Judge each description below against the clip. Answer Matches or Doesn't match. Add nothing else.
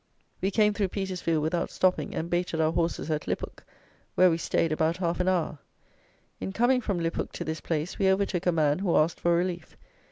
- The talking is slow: Doesn't match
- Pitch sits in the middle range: Matches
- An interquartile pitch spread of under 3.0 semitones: Matches